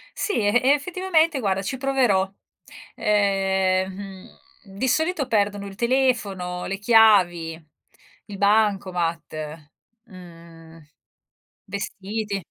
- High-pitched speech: Yes, high, 200 Hz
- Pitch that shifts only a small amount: No, average, 4.3 semitones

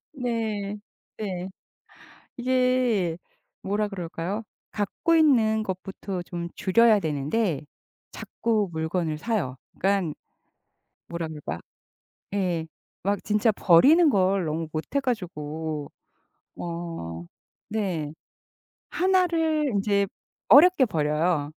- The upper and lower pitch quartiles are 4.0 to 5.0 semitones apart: No, wide, 5.6 semitones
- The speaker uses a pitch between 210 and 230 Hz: No, high, 195 Hz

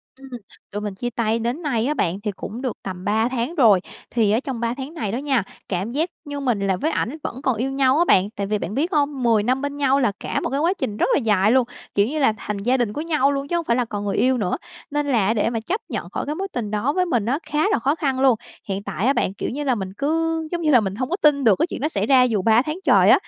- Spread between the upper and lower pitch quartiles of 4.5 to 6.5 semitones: Yes, average, 5.1 semitones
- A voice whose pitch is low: No, very high, 250 Hz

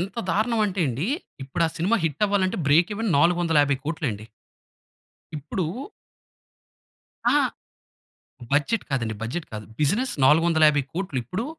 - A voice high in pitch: No, medium, 160 Hz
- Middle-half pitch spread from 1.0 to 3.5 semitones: No, average, 5.0 semitones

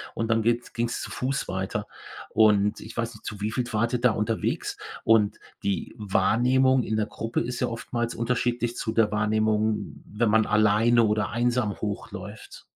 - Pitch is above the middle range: No, low, 110 Hz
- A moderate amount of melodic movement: No, narrow, 2.0 semitones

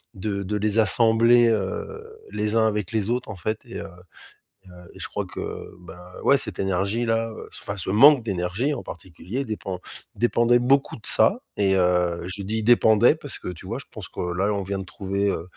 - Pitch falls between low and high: No, low, 105 Hz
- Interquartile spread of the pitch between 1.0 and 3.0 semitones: No, average, 3.5 semitones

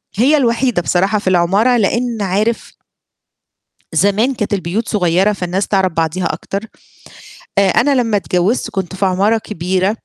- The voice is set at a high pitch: Yes, high, 200 Hz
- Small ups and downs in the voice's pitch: No, average, 3.5 semitones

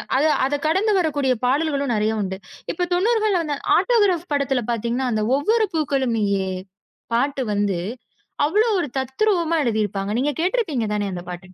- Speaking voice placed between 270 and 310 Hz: Yes, very high, 280 Hz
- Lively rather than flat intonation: Yes, wide, 7.6 semitones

